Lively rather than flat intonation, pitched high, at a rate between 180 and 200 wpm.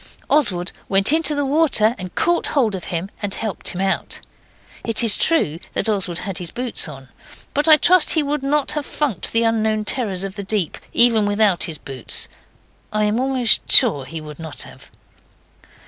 Yes: wide, 6.6 semitones; high, 215 Hz; average, 185 wpm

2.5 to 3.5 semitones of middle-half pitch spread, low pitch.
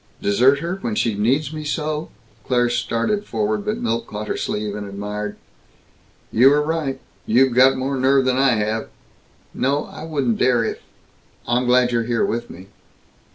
No: average, 3.9 semitones; low, 125 Hz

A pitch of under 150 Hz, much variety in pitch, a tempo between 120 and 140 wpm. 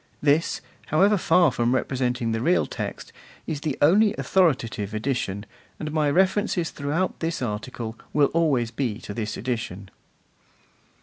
Yes: low, 135 Hz; wide, 6.2 semitones; slow, 135 wpm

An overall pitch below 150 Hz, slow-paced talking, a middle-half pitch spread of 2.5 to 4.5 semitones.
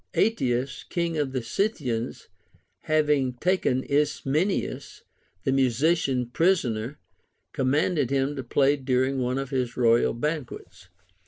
Yes: low, 135 Hz; slow, 110 wpm; average, 3.2 semitones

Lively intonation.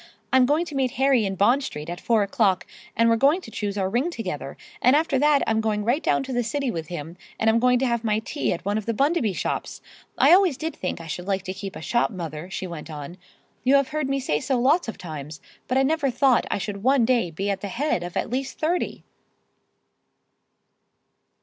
Yes: wide, 6.3 semitones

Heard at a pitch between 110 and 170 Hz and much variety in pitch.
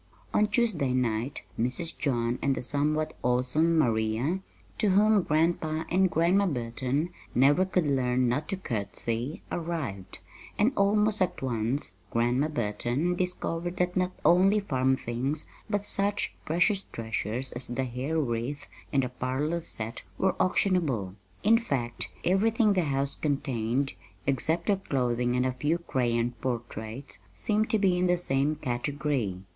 Yes: medium, 140 Hz; wide, 6.5 semitones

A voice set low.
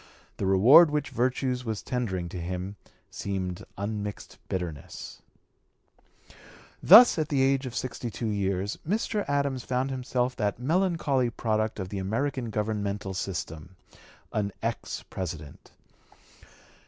Yes: low, 110 Hz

